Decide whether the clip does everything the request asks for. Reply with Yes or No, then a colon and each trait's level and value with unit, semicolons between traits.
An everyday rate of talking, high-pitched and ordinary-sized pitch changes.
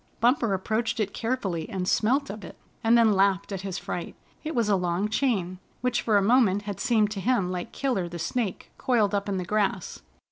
No: fast, 210 wpm; high, 205 Hz; average, 3.7 semitones